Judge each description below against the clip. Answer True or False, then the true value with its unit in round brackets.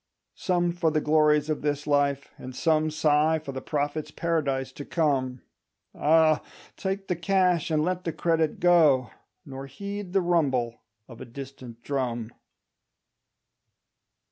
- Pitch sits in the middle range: True (150 Hz)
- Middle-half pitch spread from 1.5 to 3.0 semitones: False (3.6 semitones)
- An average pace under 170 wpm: True (140 wpm)